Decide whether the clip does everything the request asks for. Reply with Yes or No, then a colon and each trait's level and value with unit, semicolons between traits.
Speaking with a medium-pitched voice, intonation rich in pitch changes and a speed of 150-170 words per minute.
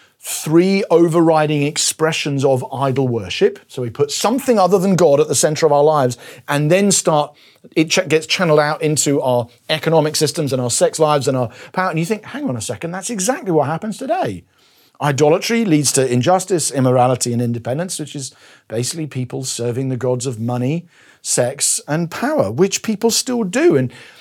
No: medium, 155 Hz; wide, 5.7 semitones; average, 185 wpm